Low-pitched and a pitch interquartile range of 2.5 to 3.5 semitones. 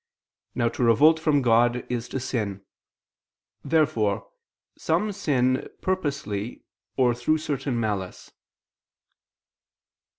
No: low, 125 Hz; average, 4.3 semitones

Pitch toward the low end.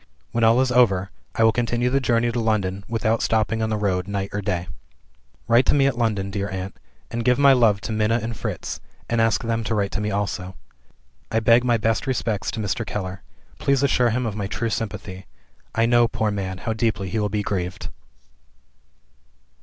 Yes: low, 110 Hz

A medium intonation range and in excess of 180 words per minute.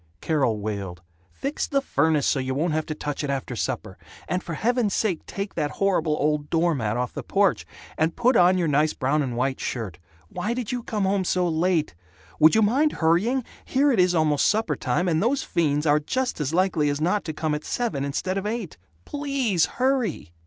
No: wide, 6.2 semitones; fast, 205 wpm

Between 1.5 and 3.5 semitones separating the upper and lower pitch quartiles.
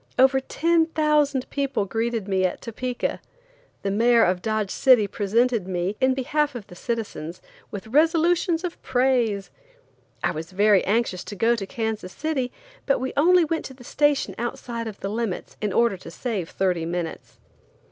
No: average, 5.2 semitones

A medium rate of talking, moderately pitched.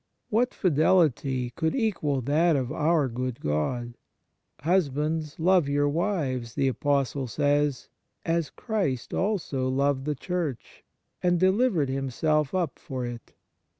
No: slow, 130 wpm; medium, 145 Hz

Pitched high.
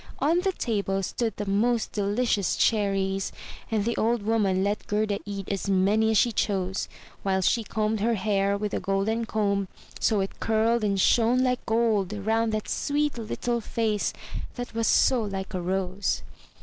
Yes: high, 210 Hz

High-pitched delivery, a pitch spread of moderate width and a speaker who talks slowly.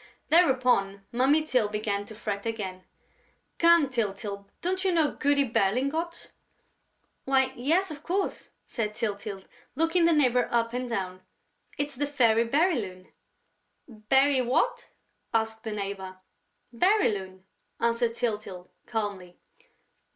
No: high, 235 Hz; wide, 5.9 semitones; slow, 115 wpm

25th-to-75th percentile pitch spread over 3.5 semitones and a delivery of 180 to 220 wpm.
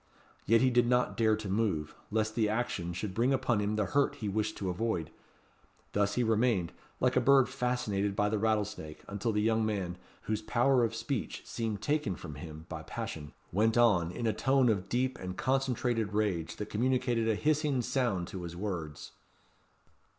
Yes: average, 3.9 semitones; average, 185 wpm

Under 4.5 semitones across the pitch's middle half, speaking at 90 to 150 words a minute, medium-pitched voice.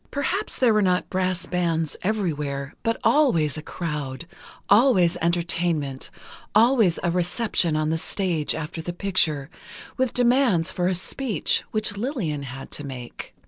No: wide, 5.6 semitones; average, 140 wpm; medium, 175 Hz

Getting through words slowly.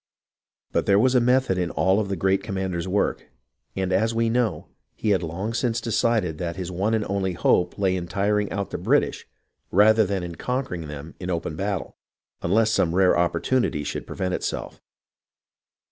No: average, 185 wpm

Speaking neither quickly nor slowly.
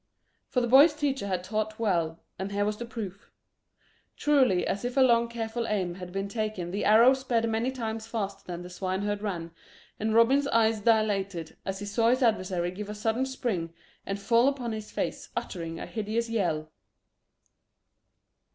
Yes: average, 175 wpm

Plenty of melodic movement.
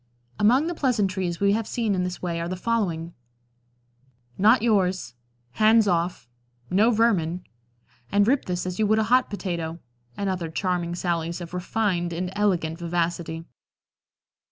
No: average, 3.8 semitones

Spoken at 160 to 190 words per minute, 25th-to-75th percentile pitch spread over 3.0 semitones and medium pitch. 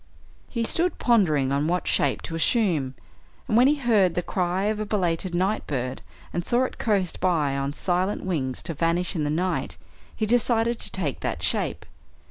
Yes: average, 185 wpm; wide, 5.6 semitones; medium, 180 Hz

